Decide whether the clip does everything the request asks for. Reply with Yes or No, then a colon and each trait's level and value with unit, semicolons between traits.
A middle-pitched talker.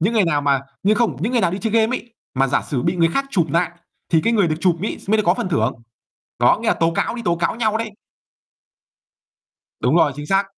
Yes: medium, 180 Hz